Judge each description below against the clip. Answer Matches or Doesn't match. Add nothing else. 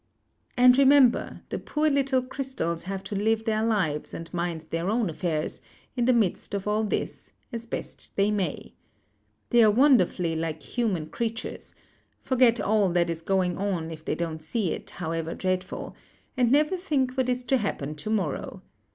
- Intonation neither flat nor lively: Doesn't match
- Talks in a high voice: Matches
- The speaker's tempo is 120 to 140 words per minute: Doesn't match